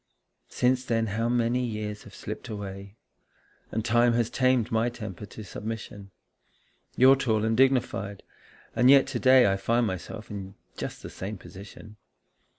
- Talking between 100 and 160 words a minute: Yes, average, 155 wpm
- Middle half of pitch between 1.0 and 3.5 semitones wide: Yes, average, 3.0 semitones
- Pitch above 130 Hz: No, low, 110 Hz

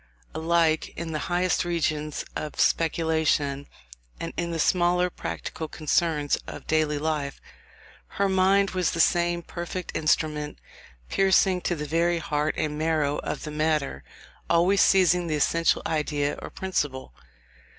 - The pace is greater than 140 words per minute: No, slow, 135 wpm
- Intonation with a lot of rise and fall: No, narrow, 2.5 semitones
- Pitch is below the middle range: No, medium, 160 Hz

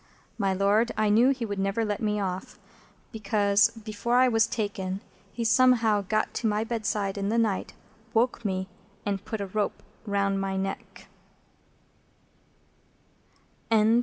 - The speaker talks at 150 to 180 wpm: No, average, 140 wpm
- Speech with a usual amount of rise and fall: No, narrow, 2.3 semitones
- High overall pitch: Yes, high, 210 Hz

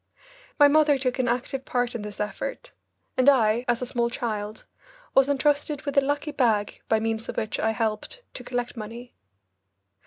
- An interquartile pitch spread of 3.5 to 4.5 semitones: Yes, average, 3.9 semitones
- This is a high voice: Yes, high, 245 Hz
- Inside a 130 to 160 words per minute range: No, average, 180 wpm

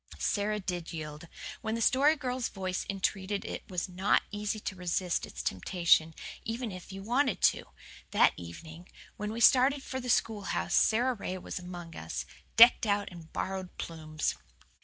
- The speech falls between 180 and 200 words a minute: No, average, 160 wpm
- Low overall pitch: No, high, 195 Hz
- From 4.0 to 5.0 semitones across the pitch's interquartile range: Yes, average, 4.4 semitones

